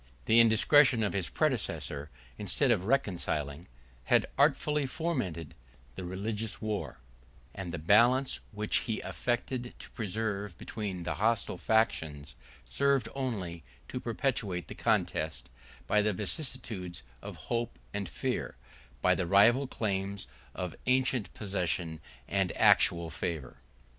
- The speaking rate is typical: No, slow, 125 wpm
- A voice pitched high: No, low, 105 Hz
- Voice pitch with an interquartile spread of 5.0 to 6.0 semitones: Yes, average, 5.3 semitones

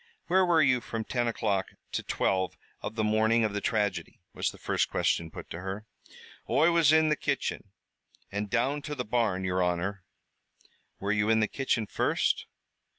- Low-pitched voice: Yes, low, 110 Hz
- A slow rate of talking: No, average, 180 wpm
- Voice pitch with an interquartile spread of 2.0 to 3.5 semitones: No, average, 4.8 semitones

